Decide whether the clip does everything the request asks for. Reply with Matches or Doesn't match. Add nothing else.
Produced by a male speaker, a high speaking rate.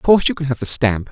Matches